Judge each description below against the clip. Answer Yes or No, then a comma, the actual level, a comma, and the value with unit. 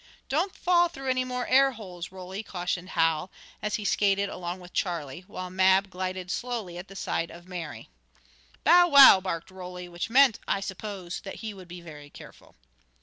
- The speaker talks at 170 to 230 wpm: Yes, average, 180 wpm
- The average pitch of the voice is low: No, high, 190 Hz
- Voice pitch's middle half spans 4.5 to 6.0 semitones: No, average, 4.1 semitones